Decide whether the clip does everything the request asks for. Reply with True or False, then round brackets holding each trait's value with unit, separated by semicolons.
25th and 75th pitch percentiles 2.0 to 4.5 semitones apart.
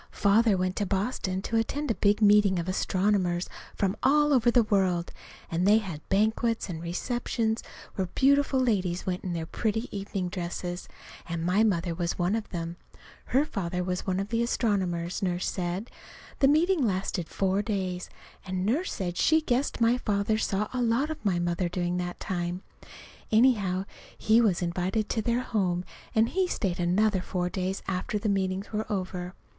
True (3.8 semitones)